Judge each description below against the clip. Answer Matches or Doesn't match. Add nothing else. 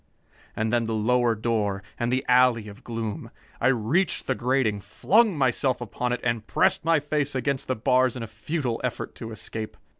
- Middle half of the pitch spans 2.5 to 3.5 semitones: Matches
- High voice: Doesn't match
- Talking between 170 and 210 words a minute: Matches